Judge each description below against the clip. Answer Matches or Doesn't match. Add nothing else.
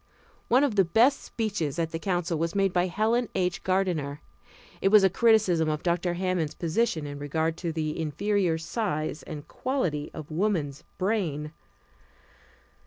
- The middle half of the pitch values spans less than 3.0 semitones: Doesn't match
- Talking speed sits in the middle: Matches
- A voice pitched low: Doesn't match